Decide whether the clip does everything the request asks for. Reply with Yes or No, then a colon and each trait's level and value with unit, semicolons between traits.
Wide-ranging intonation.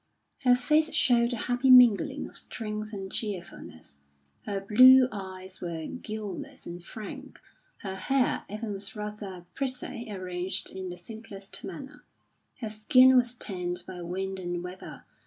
No: average, 4.7 semitones